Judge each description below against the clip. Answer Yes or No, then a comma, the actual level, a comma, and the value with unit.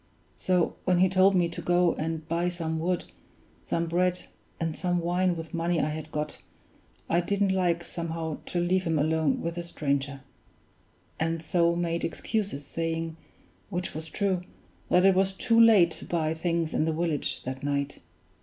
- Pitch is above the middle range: No, medium, 170 Hz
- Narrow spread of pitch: Yes, narrow, 2.0 semitones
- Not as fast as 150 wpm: No, average, 175 wpm